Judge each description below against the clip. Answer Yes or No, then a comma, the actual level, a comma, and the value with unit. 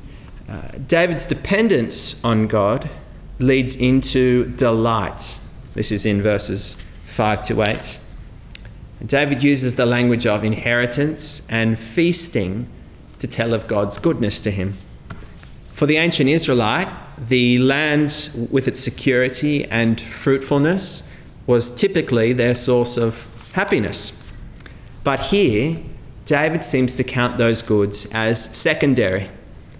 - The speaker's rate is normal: No, slow, 115 wpm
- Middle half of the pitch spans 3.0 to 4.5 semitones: Yes, average, 4.1 semitones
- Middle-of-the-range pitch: No, low, 120 Hz